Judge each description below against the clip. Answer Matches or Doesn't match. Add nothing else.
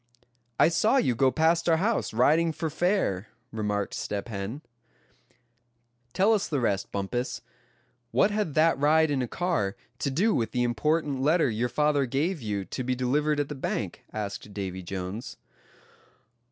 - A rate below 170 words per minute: Matches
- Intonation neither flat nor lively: Doesn't match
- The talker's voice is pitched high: Doesn't match